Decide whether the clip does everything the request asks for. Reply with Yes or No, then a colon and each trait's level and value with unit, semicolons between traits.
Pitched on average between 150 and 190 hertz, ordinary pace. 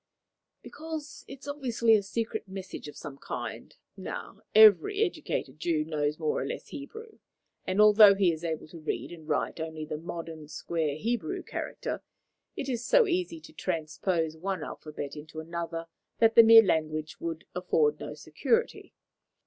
Yes: medium, 185 Hz; average, 160 wpm